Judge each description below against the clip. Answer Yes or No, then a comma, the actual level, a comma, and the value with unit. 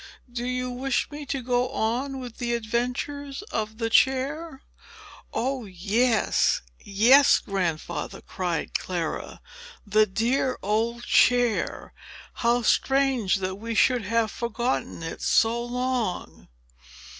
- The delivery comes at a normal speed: No, slow, 115 wpm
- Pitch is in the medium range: No, high, 235 Hz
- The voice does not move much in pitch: No, average, 3.1 semitones